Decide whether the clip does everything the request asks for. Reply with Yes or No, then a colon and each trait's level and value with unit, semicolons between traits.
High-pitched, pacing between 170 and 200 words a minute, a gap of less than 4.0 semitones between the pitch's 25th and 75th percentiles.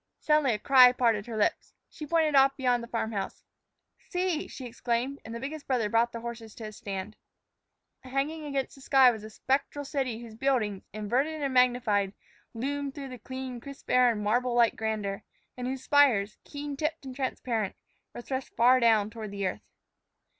Yes: very high, 250 Hz; average, 185 wpm; average, 3.6 semitones